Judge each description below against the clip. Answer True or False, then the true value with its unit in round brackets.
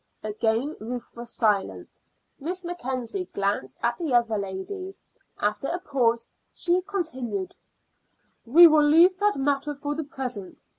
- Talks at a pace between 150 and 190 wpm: False (135 wpm)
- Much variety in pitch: True (7.0 semitones)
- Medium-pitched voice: False (265 Hz)